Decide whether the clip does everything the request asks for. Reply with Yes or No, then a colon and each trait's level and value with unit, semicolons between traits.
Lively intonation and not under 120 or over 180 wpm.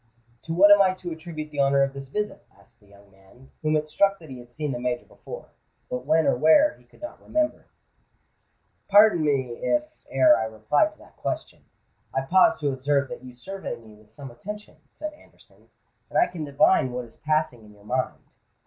No: wide, 7.2 semitones; fast, 205 wpm